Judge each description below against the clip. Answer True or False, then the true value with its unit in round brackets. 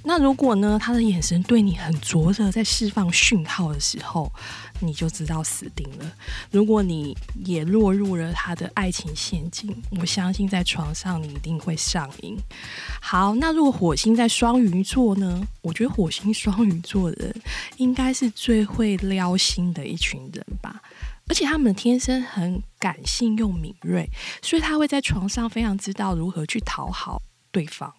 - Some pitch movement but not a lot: True (4.8 semitones)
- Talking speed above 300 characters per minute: False (250 characters per minute)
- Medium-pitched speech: False (195 Hz)